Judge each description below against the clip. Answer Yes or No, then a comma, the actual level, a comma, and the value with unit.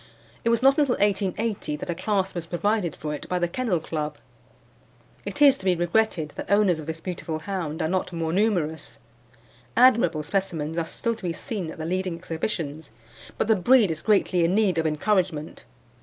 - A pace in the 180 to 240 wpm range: Yes, average, 190 wpm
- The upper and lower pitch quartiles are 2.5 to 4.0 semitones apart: No, average, 4.5 semitones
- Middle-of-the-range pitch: Yes, medium, 180 Hz